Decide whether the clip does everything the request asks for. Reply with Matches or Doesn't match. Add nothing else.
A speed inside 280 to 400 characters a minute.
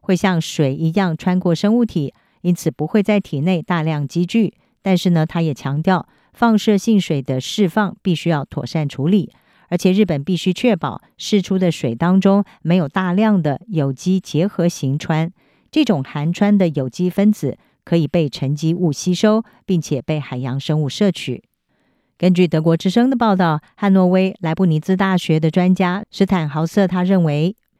Doesn't match